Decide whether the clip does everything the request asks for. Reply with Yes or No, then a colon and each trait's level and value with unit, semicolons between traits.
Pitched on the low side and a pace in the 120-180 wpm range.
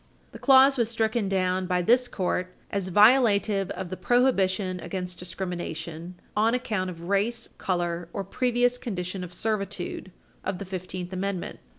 No: high, 190 Hz; average, 150 wpm